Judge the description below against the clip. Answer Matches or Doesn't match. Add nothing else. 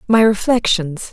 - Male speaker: Doesn't match